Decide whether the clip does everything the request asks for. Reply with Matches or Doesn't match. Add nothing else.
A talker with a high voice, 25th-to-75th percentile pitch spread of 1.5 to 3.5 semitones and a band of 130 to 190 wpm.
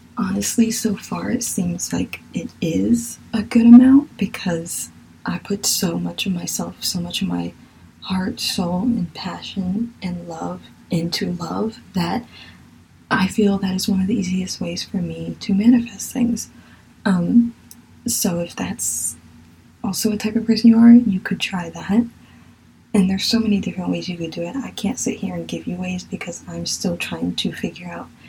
Doesn't match